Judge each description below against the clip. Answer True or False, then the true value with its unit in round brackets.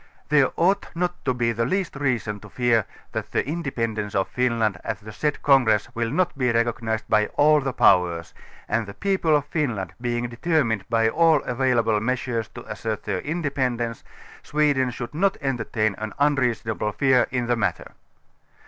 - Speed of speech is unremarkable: True (165 wpm)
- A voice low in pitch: True (120 Hz)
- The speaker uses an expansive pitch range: False (4.5 semitones)